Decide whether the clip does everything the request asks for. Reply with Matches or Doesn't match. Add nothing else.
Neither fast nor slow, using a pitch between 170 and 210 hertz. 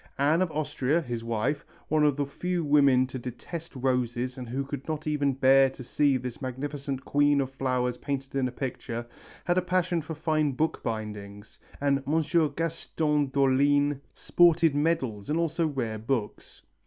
Doesn't match